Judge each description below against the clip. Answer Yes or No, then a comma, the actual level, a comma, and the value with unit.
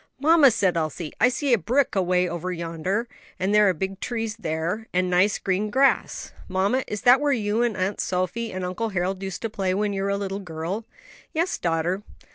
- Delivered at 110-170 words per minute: No, fast, 205 wpm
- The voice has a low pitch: No, high, 195 Hz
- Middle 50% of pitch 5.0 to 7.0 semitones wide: No, average, 3.9 semitones